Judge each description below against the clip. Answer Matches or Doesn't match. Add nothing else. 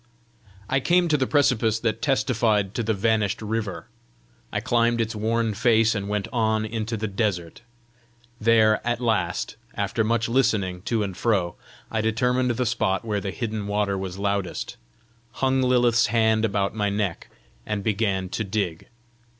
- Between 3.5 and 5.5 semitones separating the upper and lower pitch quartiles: Doesn't match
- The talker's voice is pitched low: Matches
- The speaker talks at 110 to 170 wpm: Matches